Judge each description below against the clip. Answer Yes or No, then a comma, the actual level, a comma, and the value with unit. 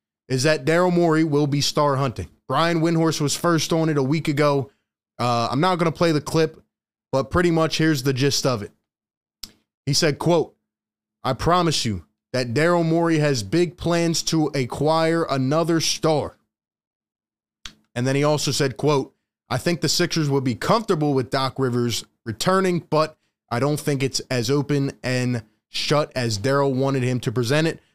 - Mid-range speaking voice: Yes, medium, 145 Hz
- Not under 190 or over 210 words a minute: No, average, 175 wpm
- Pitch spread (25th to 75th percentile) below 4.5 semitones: Yes, average, 4.1 semitones